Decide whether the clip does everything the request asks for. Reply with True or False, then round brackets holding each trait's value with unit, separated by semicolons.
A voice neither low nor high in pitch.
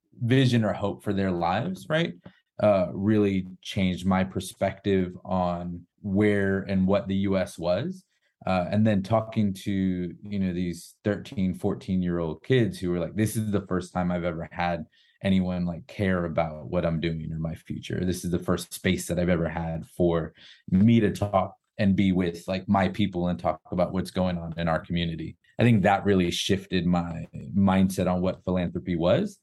False (95 Hz)